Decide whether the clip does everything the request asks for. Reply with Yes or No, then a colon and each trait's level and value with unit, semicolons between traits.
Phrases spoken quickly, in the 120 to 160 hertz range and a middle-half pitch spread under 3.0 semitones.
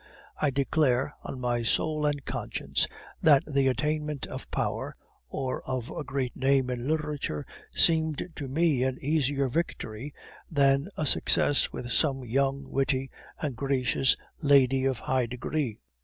No: average, 140 wpm; low, 135 Hz; narrow, 2.4 semitones